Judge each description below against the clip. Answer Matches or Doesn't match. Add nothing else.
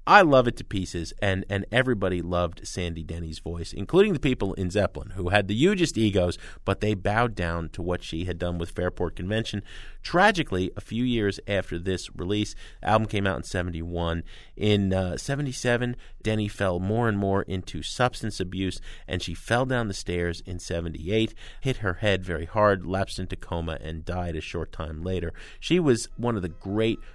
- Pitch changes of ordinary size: Matches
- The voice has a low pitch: Matches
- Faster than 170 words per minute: Matches